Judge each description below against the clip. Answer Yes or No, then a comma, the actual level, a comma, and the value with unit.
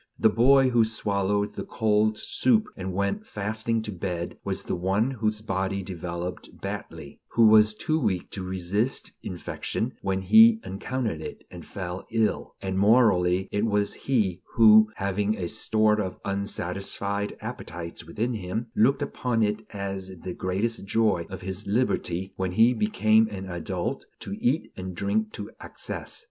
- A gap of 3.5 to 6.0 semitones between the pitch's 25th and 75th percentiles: No, average, 2.9 semitones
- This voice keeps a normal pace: Yes, average, 155 wpm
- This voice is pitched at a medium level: No, low, 105 Hz